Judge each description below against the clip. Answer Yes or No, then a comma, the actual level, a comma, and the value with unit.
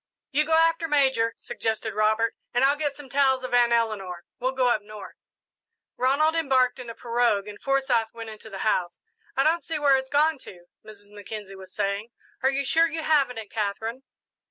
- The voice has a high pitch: Yes, high, 245 Hz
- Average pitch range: Yes, average, 4.4 semitones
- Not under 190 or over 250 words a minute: Yes, average, 195 wpm